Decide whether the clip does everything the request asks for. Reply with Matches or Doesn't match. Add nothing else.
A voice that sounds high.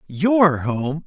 Doesn't match